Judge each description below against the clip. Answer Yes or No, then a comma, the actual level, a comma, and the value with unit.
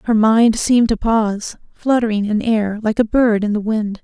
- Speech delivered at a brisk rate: Yes, fast, 210 wpm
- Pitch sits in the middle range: No, high, 220 Hz